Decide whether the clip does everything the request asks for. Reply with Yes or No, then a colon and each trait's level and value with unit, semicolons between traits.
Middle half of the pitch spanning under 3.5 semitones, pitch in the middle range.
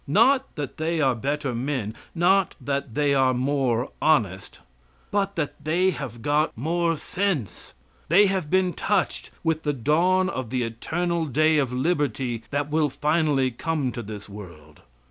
No: average, 5.1 semitones; medium, 145 Hz